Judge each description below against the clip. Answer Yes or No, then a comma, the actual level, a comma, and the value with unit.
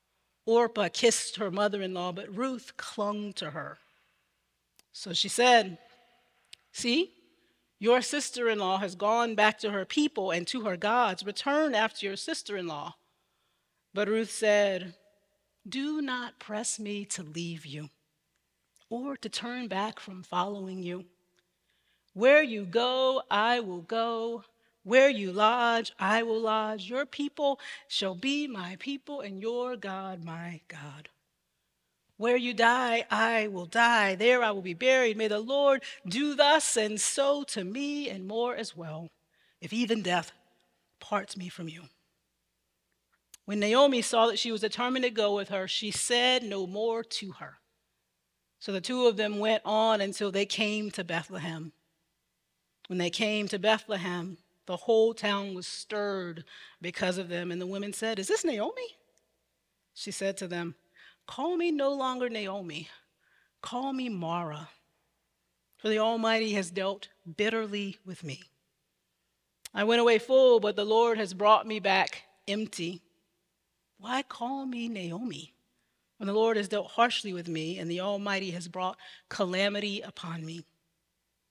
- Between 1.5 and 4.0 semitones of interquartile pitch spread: No, average, 4.5 semitones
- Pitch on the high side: Yes, high, 205 Hz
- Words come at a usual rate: Yes, average, 150 wpm